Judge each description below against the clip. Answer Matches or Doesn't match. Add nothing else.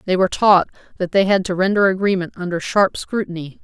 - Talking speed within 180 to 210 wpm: Matches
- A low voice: Doesn't match